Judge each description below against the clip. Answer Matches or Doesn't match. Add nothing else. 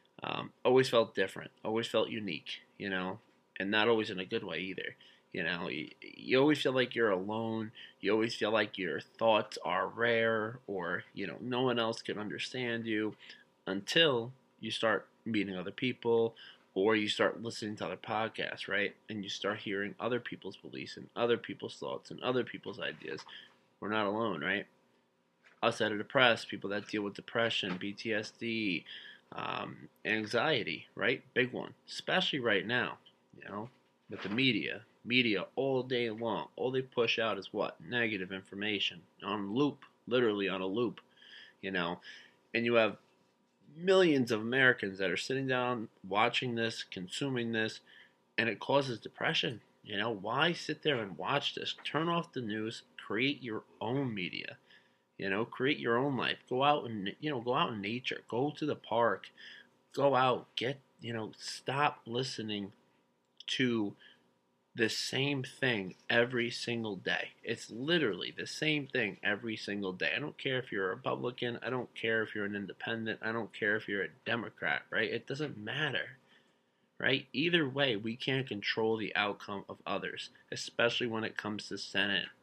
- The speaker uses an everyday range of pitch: Matches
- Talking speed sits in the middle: Matches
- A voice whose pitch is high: Doesn't match